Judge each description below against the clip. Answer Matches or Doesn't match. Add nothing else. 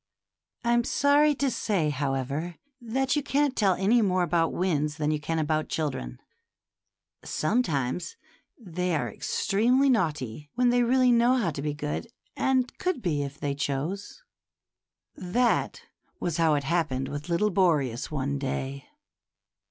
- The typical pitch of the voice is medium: Matches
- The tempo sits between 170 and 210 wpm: Doesn't match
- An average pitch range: Doesn't match